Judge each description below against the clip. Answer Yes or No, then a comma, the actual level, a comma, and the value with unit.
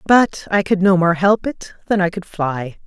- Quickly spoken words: Yes, fast, 230 wpm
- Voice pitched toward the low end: No, medium, 185 Hz